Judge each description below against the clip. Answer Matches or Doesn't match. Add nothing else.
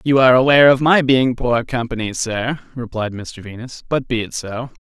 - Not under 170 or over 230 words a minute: Matches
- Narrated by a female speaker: Doesn't match